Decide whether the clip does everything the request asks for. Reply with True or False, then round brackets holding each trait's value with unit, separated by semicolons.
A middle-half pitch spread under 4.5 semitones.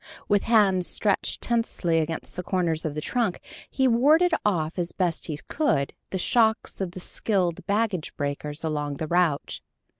False (5.6 semitones)